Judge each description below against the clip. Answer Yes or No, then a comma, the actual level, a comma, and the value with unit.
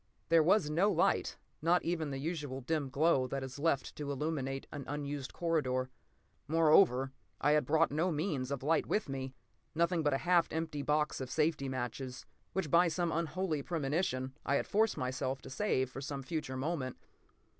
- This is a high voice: No, medium, 150 Hz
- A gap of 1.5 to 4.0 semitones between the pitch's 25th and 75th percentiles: Yes, average, 3.6 semitones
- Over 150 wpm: Yes, average, 175 wpm